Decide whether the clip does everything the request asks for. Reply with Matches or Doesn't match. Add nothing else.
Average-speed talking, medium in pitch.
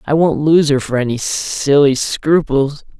Matches